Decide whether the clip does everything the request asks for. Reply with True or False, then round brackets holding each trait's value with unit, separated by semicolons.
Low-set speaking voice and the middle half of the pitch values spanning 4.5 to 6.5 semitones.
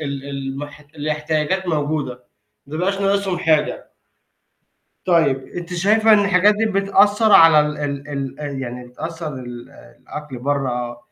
False (150 Hz; 4.9 semitones)